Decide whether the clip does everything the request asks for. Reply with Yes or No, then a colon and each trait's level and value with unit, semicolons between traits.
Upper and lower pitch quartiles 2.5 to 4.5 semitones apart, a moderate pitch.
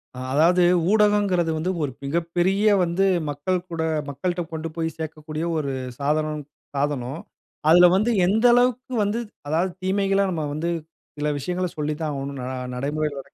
Yes: average, 3.8 semitones; medium, 165 Hz